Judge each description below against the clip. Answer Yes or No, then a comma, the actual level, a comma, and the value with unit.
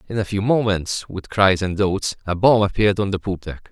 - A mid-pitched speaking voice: No, low, 100 Hz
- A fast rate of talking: Yes, fast, 240 wpm